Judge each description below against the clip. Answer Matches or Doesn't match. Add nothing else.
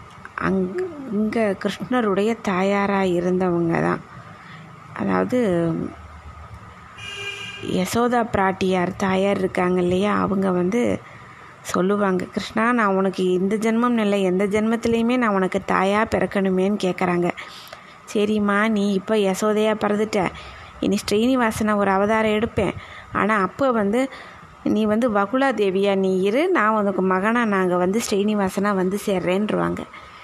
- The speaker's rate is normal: Matches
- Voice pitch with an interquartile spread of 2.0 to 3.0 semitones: Matches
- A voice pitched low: Doesn't match